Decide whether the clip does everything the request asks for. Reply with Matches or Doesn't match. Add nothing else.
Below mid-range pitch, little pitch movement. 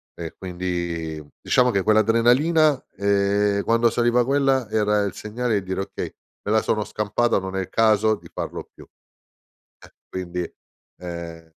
Doesn't match